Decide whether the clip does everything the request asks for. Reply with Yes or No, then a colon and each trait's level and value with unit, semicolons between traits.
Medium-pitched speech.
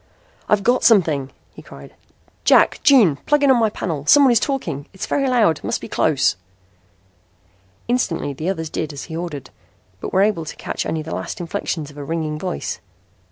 Yes: medium, 170 Hz